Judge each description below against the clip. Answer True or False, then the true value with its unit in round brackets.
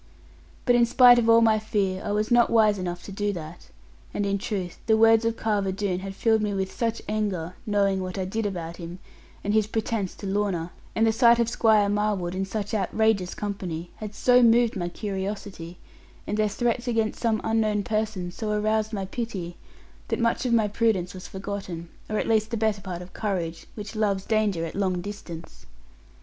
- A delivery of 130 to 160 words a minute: False (200 wpm)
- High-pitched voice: True (205 Hz)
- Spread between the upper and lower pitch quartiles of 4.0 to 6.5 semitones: False (2.8 semitones)